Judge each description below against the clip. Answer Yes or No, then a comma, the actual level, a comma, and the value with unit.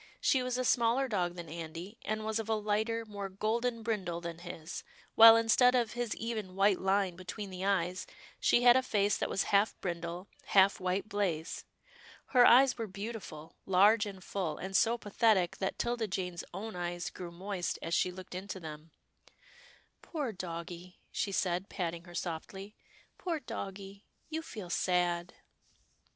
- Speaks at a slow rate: No, average, 175 wpm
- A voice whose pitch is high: Yes, high, 195 Hz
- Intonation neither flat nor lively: Yes, average, 4.0 semitones